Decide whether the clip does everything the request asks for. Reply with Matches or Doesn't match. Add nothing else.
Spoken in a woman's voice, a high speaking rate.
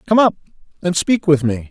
Doesn't match